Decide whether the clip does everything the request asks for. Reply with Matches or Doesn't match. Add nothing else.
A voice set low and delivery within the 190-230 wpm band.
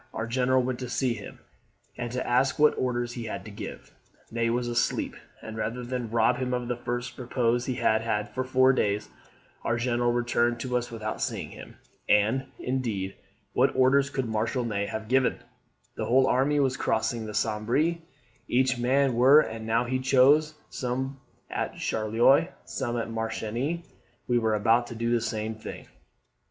Doesn't match